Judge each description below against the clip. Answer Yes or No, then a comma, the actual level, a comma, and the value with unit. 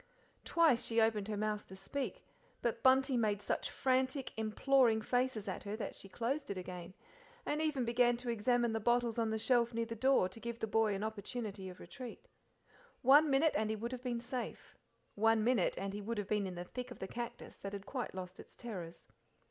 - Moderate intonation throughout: Yes, average, 3.4 semitones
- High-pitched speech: Yes, high, 230 Hz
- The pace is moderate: No, fast, 210 wpm